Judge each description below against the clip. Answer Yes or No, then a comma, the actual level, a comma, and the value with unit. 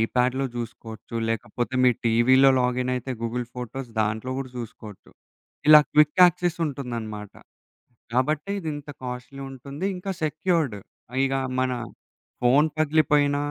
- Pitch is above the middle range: No, low, 130 Hz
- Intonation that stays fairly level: No, average, 3.6 semitones